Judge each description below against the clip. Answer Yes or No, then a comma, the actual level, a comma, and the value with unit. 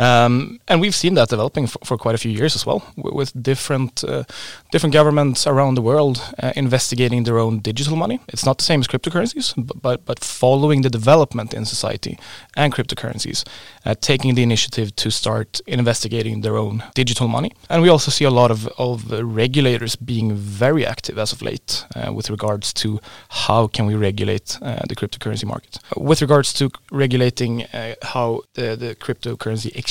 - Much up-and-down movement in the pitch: No, average, 3.8 semitones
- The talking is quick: No, average, 195 wpm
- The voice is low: Yes, low, 125 Hz